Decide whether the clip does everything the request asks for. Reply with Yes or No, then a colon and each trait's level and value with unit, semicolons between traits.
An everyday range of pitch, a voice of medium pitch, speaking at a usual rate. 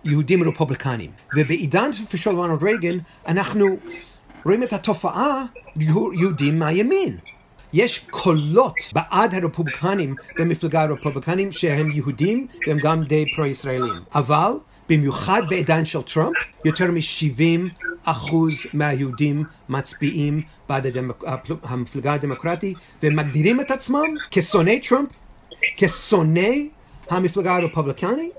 No: average, 4.6 semitones; medium, 165 Hz; slow, 95 wpm